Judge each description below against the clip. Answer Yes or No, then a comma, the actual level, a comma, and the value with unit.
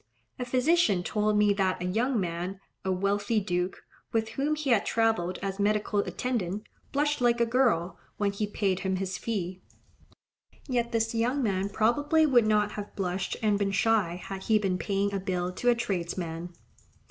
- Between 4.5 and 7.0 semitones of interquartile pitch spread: No, average, 3.7 semitones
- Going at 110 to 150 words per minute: No, average, 175 wpm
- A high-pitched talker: Yes, high, 205 Hz